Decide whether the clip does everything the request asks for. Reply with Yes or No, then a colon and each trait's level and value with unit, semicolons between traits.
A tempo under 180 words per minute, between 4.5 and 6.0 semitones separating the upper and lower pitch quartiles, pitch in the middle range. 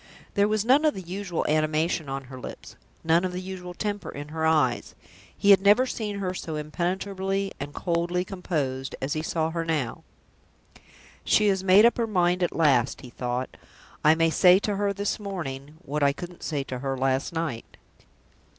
No: average, 185 wpm; average, 5.0 semitones; medium, 170 Hz